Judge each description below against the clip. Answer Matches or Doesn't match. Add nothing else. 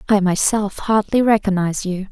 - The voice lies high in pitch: Matches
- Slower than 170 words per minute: Matches